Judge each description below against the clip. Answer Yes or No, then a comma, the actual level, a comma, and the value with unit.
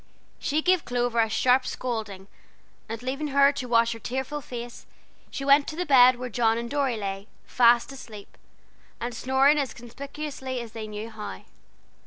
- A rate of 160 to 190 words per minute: Yes, average, 170 wpm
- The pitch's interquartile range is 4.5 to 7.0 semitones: No, average, 3.3 semitones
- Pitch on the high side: Yes, high, 245 Hz